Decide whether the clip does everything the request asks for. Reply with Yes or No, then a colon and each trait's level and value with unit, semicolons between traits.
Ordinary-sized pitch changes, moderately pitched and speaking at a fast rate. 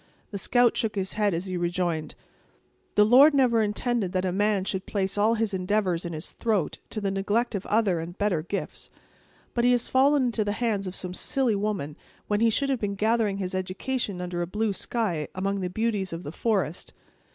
No: average, 3.6 semitones; high, 205 Hz; fast, 210 wpm